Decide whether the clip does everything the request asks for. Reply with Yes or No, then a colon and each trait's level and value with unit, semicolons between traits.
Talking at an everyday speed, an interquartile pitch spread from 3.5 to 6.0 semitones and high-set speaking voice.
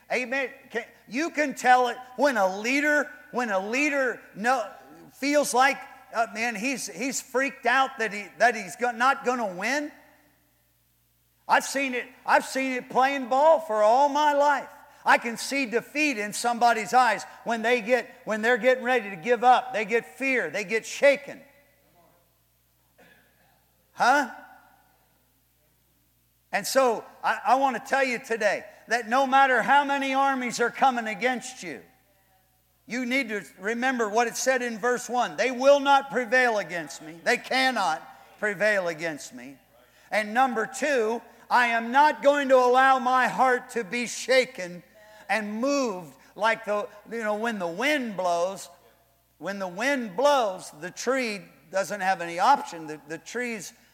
Yes: average, 160 wpm; average, 4.3 semitones; high, 245 Hz